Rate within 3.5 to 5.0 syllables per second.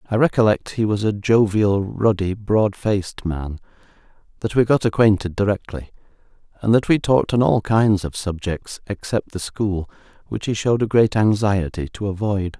Yes: 4.9 syllables/s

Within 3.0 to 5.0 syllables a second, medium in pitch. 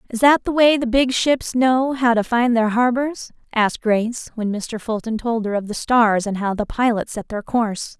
No: 4.8 syllables/s; high, 235 Hz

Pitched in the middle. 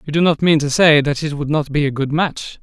Yes: medium, 150 Hz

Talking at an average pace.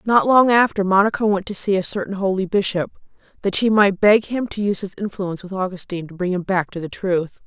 No: fast, 235 wpm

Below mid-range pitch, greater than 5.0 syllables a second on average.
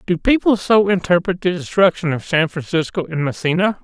No: medium, 175 Hz; 5.5 syllables/s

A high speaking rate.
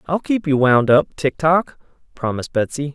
No: average, 185 wpm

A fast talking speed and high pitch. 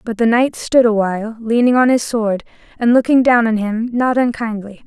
Yes: fast, 210 wpm; high, 230 Hz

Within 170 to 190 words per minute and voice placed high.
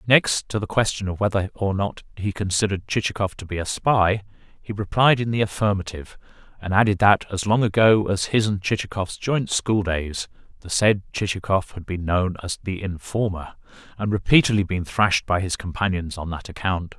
No: average, 180 wpm; low, 100 Hz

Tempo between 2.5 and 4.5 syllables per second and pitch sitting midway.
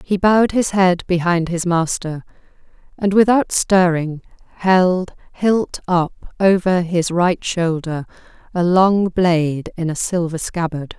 Yes: 3.8 syllables/s; medium, 180 Hz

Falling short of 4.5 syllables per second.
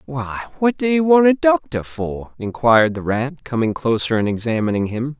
No: 5.0 syllables/s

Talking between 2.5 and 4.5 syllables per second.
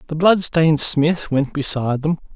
No: 5.0 syllables/s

